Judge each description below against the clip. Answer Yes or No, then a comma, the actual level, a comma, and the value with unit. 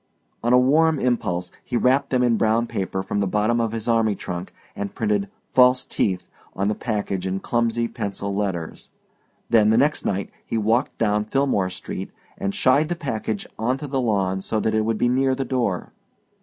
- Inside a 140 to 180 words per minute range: No, average, 190 wpm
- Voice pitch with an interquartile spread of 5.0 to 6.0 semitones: No, average, 4.1 semitones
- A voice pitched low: Yes, low, 115 Hz